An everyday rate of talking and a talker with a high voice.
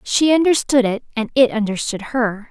Yes: average, 170 wpm; high, 240 Hz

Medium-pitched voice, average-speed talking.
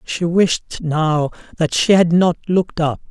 Yes: medium, 170 Hz; average, 175 wpm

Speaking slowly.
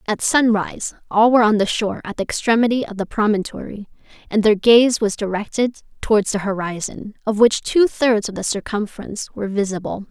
No: average, 180 wpm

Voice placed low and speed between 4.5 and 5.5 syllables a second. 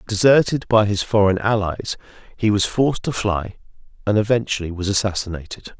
Yes: low, 105 Hz; 5.4 syllables/s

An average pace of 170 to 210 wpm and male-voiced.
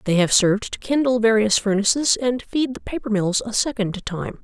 No: fast, 205 wpm; female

